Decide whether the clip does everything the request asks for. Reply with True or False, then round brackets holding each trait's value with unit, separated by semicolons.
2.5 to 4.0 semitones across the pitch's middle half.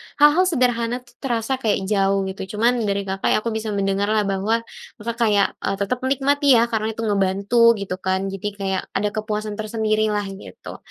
True (2.9 semitones)